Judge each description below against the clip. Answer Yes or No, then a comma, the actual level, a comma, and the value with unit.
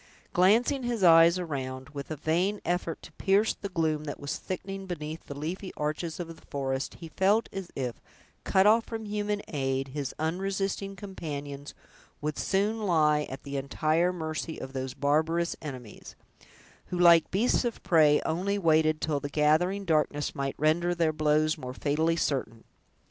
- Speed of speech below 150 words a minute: No, average, 165 wpm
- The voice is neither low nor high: Yes, medium, 160 Hz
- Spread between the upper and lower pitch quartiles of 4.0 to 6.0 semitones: Yes, average, 4.4 semitones